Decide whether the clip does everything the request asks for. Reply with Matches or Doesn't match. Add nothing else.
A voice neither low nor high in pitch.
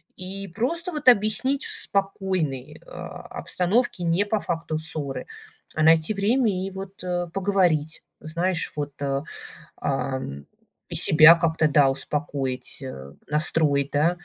Matches